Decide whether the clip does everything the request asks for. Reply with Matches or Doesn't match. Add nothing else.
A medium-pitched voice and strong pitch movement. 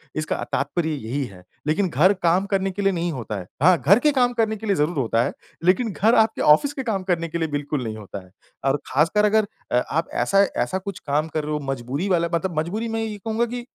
Matches